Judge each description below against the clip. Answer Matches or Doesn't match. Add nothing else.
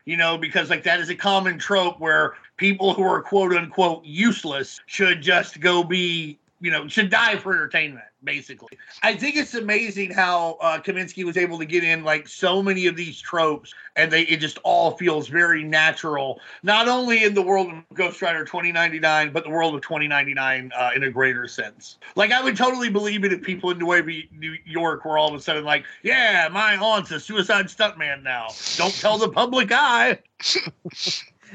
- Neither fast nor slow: Matches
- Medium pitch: Matches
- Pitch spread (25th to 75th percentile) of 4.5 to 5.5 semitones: Doesn't match